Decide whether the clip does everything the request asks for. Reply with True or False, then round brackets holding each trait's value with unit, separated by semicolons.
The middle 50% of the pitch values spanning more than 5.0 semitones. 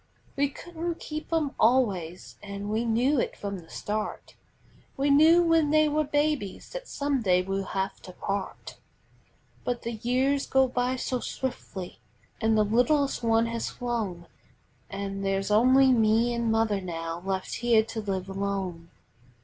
True (5.6 semitones)